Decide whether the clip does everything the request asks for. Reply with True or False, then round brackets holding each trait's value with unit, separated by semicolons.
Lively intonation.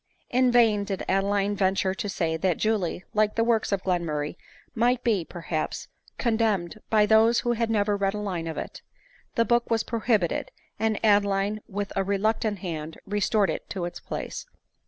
False (2.8 semitones)